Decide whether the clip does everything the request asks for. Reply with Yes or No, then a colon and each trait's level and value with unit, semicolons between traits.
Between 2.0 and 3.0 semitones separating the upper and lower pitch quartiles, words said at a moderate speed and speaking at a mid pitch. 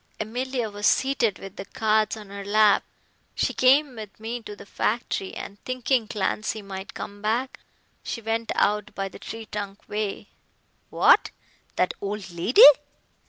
No: narrow, 2.4 semitones; average, 155 wpm; high, 215 Hz